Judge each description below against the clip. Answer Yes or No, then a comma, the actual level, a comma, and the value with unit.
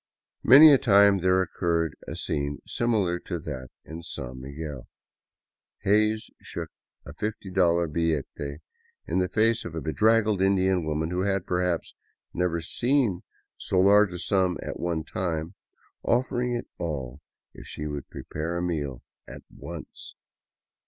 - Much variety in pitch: No, average, 4.2 semitones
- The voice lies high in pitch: No, very low, 90 Hz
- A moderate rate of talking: Yes, average, 145 wpm